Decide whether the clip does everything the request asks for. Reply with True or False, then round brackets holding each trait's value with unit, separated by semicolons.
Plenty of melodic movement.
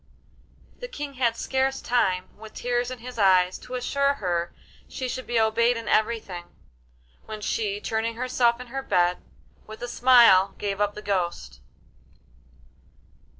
False (4.1 semitones)